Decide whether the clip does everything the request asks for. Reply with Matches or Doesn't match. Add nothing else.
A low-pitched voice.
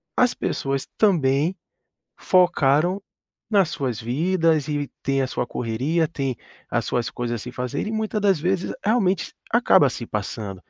Doesn't match